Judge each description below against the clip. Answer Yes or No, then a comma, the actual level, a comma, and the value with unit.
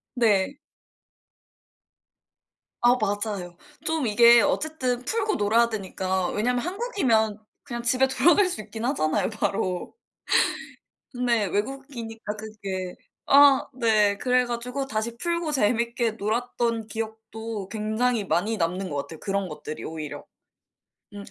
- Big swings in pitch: No, average, 3.5 semitones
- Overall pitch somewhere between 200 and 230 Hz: Yes, high, 225 Hz